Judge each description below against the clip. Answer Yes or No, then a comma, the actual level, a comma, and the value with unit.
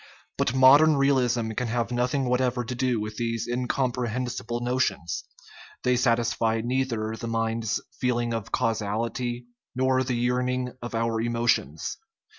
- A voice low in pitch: Yes, low, 120 Hz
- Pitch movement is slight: Yes, narrow, 1.7 semitones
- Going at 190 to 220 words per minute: No, average, 140 wpm